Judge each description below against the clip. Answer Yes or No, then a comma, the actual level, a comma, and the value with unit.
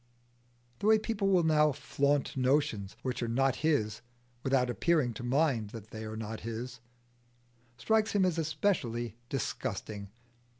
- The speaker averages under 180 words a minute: Yes, average, 140 wpm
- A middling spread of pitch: No, wide, 5.7 semitones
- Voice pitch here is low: Yes, low, 130 Hz